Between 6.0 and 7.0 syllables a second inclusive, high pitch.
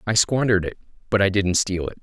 No: 6.4 syllables/s; low, 100 Hz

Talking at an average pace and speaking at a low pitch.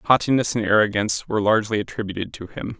Yes: average, 170 wpm; low, 105 Hz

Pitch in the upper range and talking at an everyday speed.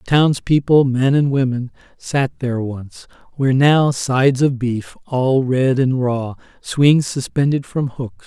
No: low, 130 Hz; average, 145 wpm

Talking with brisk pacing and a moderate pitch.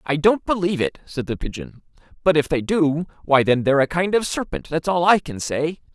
Yes: fast, 230 wpm; medium, 160 Hz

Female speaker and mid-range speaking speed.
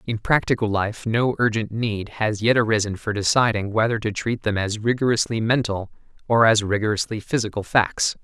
No: male; average, 170 wpm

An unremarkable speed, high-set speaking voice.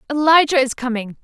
Yes: average, 145 wpm; very high, 270 Hz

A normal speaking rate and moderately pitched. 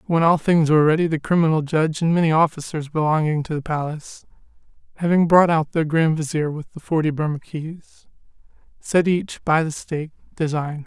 Yes: average, 180 wpm; medium, 155 Hz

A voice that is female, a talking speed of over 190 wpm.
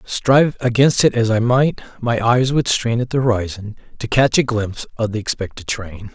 No: male; fast, 205 wpm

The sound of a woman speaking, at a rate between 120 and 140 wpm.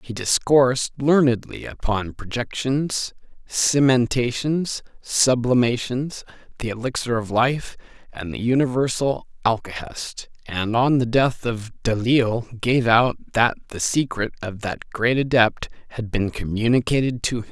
No: male; slow, 135 wpm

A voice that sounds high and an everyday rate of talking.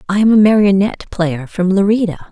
Yes: high, 195 Hz; average, 180 wpm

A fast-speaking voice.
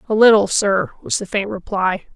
No: average, 195 wpm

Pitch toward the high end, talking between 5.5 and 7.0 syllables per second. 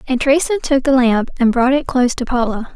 Yes: very high, 255 Hz; 6.3 syllables/s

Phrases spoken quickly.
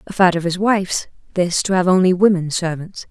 Yes: fast, 210 wpm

